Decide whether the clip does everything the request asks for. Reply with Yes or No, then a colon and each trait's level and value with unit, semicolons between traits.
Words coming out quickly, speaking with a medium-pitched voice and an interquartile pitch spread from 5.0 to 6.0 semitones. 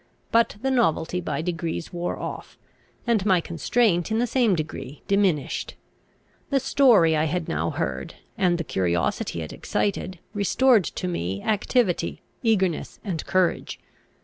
No: average, 140 wpm; medium, 180 Hz; average, 5.3 semitones